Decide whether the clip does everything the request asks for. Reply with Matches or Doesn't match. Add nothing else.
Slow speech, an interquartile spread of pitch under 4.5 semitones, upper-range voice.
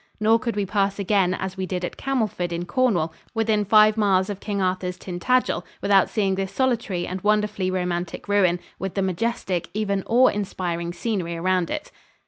Doesn't match